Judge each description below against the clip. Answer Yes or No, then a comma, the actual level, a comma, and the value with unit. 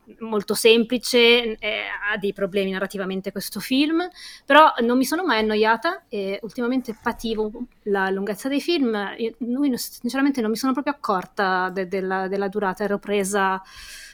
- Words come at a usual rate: Yes, average, 155 wpm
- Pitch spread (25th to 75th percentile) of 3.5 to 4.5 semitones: Yes, average, 4.0 semitones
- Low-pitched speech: No, high, 220 Hz